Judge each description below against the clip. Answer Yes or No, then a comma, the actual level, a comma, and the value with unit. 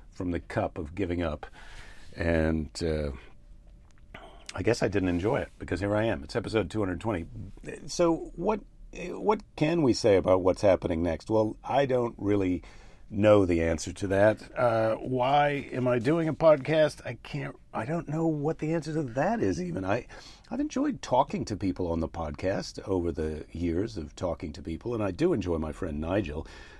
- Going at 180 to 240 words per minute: Yes, average, 190 wpm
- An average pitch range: No, wide, 8.9 semitones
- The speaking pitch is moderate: No, low, 105 Hz